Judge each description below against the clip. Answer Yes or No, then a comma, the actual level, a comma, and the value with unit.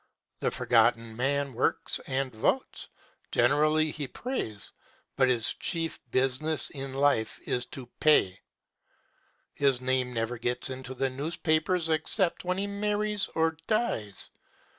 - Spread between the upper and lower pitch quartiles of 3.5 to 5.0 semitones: Yes, average, 4.5 semitones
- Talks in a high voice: No, low, 135 Hz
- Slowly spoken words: Yes, slow, 125 wpm